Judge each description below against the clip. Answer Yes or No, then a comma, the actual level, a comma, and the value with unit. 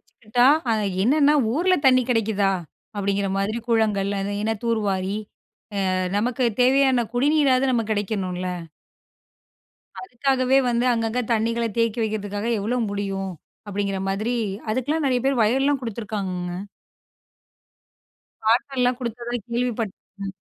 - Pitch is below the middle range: No, high, 230 Hz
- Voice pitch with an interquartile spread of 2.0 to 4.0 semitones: Yes, average, 3.7 semitones